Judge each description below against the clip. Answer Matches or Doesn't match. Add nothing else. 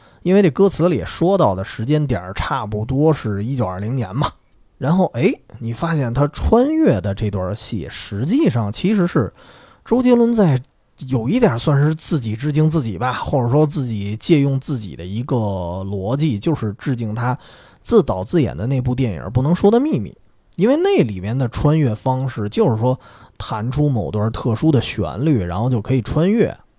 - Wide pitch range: Matches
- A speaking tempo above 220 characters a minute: Matches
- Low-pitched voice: Matches